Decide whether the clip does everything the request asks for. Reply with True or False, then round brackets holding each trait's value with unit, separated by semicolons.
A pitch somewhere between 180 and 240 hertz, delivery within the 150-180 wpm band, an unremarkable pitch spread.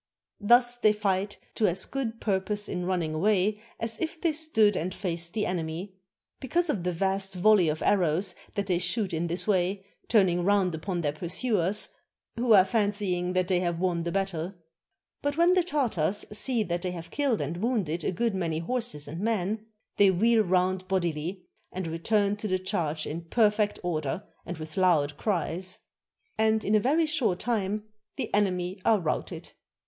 True (190 Hz; 175 wpm; 3.7 semitones)